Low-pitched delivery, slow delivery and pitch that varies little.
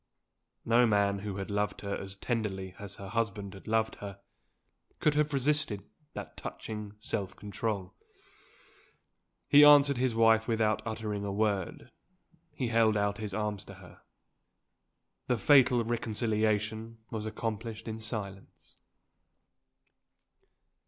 Yes: low, 110 Hz; slow, 125 wpm; narrow, 2.1 semitones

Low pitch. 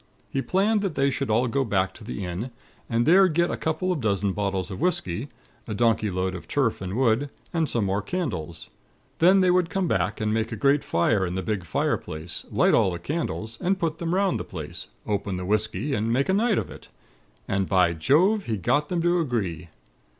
Yes: low, 115 Hz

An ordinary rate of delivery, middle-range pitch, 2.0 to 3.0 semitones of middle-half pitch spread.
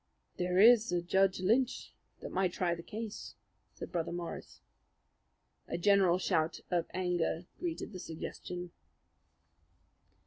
No: slow, 125 wpm; medium, 180 Hz; narrow, 2.5 semitones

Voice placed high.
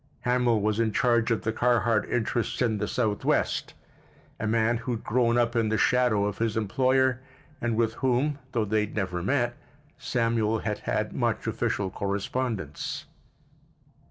No: low, 115 Hz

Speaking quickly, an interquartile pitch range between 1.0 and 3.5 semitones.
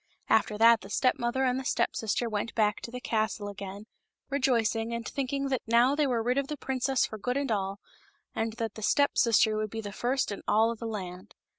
Yes: fast, 230 wpm; average, 3.2 semitones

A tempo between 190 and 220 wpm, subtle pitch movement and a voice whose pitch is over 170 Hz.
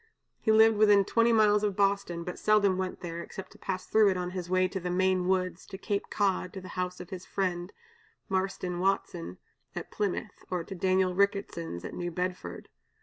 Yes: average, 200 wpm; narrow, 1.9 semitones; medium, 185 Hz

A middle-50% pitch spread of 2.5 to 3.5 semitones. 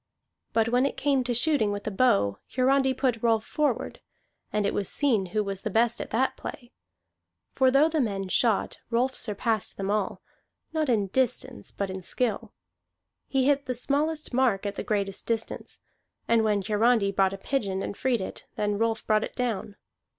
No: average, 4.3 semitones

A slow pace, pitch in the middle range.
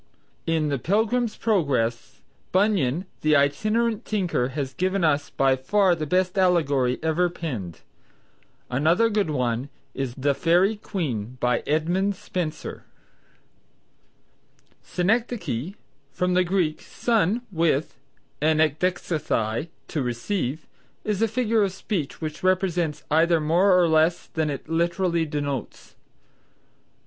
Yes: slow, 115 wpm; medium, 165 Hz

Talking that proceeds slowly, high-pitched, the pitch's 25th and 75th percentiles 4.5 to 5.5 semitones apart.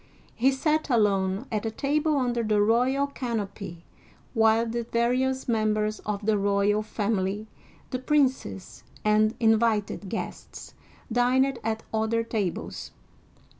No: slow, 120 wpm; high, 225 Hz; average, 3.1 semitones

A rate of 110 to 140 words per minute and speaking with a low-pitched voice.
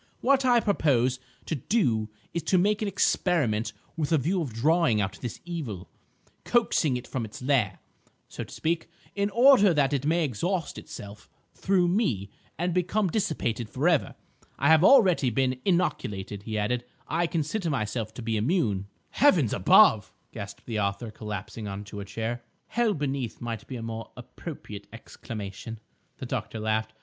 No: average, 165 wpm; low, 130 Hz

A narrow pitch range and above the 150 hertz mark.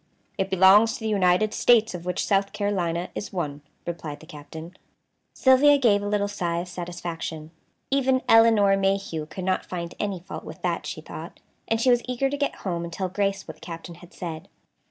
No: average, 3.9 semitones; high, 190 Hz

